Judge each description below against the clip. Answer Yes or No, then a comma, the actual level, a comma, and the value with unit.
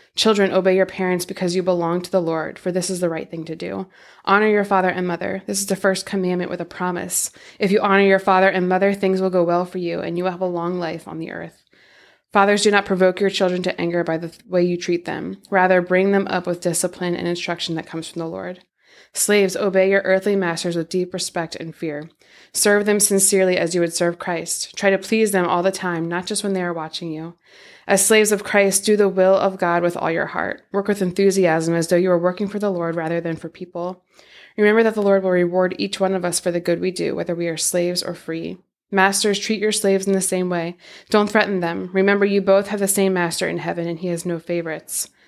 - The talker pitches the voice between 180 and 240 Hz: Yes, medium, 185 Hz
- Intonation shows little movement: Yes, narrow, 2.2 semitones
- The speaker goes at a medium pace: No, fast, 250 wpm